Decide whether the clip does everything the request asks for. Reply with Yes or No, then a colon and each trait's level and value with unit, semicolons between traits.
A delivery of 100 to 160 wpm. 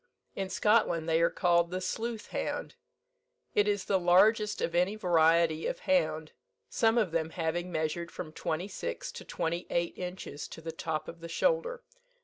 No: average, 170 wpm